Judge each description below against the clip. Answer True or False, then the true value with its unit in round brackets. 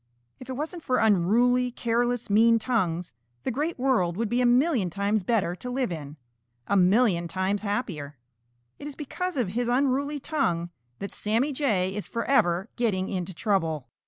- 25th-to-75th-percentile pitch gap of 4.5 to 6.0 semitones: True (5.4 semitones)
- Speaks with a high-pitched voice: True (225 Hz)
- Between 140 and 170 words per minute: True (165 wpm)